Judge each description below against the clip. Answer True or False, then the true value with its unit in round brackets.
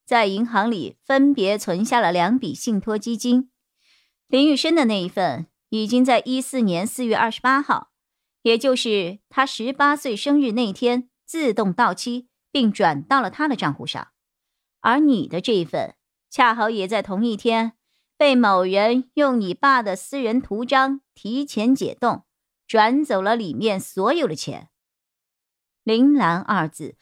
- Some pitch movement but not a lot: True (4.1 semitones)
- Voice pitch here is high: True (235 Hz)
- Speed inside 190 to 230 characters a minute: True (220 characters per minute)